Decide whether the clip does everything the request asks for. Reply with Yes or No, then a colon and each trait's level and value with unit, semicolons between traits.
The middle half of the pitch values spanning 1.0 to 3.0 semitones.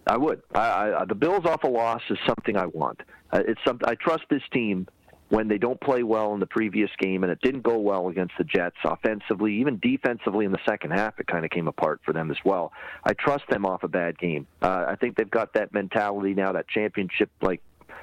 No: average, 3.9 semitones